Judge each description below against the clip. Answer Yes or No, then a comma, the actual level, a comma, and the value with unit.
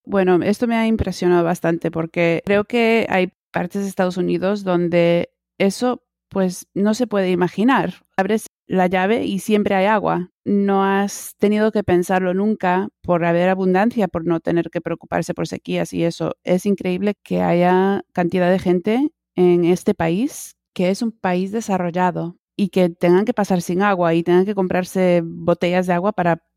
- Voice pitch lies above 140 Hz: Yes, medium, 185 Hz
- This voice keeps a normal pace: Yes, average, 170 wpm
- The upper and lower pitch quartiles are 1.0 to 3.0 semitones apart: Yes, narrow, 2.5 semitones